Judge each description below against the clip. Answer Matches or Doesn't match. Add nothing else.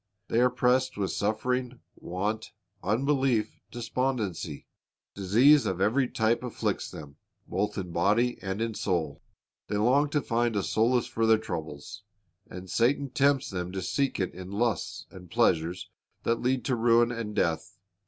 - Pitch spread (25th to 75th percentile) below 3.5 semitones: Doesn't match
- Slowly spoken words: Doesn't match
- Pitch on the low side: Matches